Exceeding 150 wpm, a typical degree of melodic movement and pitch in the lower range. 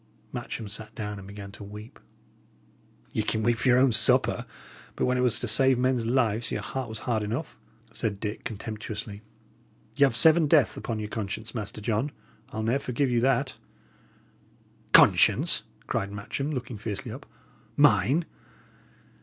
Yes: average, 160 wpm; average, 3.5 semitones; low, 115 Hz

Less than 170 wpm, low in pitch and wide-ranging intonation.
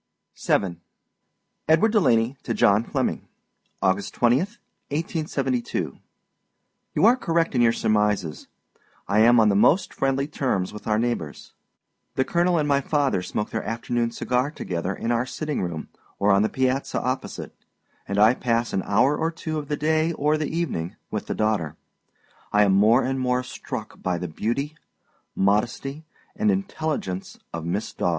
Yes: average, 160 wpm; low, 120 Hz; wide, 6.3 semitones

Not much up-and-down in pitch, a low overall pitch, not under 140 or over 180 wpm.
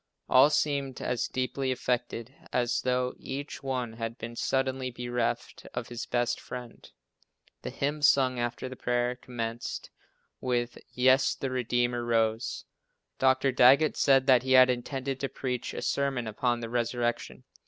Yes: narrow, 1.6 semitones; low, 125 Hz; average, 145 wpm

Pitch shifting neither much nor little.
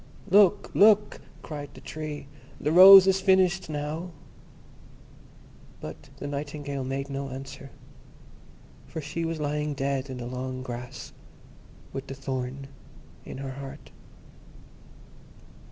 Yes: average, 3.3 semitones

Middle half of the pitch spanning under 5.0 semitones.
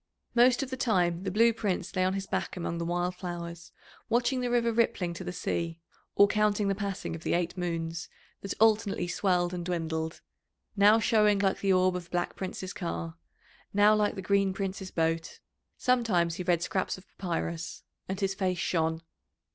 Yes: average, 3.2 semitones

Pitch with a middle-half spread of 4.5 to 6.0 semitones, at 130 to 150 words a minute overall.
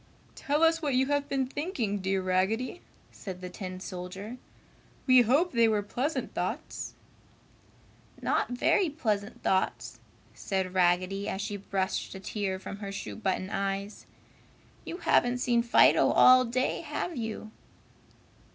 Yes: average, 5.0 semitones; average, 140 wpm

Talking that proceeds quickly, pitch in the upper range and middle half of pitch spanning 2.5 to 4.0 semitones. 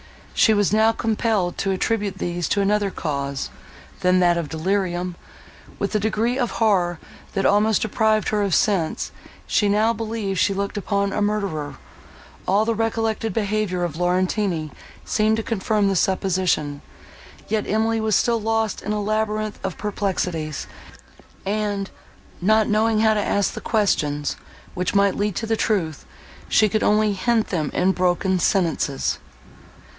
No: average, 150 wpm; high, 205 Hz; average, 3.0 semitones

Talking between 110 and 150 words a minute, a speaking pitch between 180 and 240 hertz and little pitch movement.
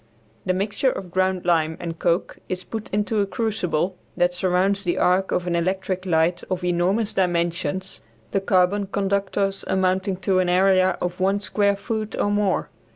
No: average, 165 wpm; medium, 185 Hz; narrow, 2.0 semitones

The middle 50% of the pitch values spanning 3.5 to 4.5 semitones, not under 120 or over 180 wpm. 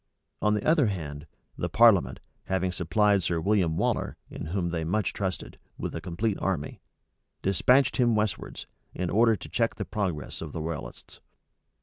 Yes: average, 4.2 semitones; average, 160 wpm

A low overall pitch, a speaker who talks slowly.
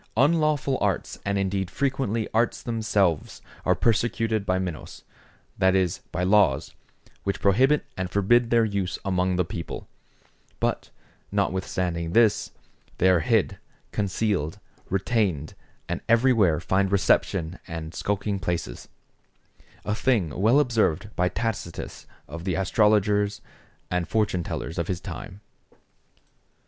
Yes: low, 100 Hz; slow, 120 wpm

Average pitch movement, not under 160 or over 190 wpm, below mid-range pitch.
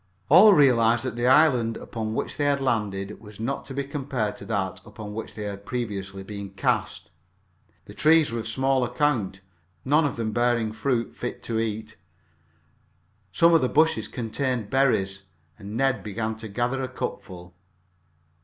Yes: average, 4.3 semitones; average, 165 wpm; low, 115 Hz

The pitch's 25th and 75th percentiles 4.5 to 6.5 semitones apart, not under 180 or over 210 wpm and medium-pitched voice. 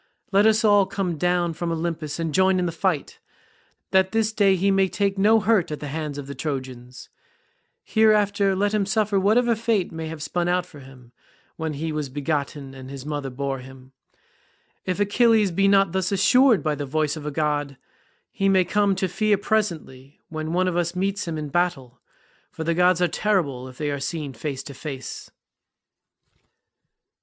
Yes: average, 5.2 semitones; average, 185 wpm; medium, 170 Hz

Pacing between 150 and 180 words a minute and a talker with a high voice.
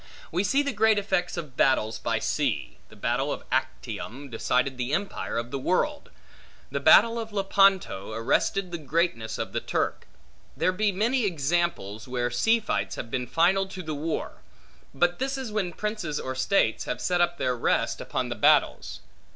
No: average, 175 wpm; medium, 175 Hz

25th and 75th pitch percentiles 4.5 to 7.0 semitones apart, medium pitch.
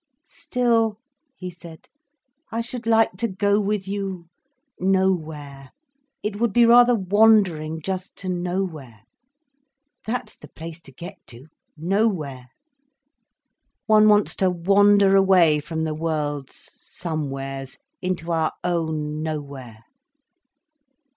Yes: average, 4.9 semitones; medium, 180 Hz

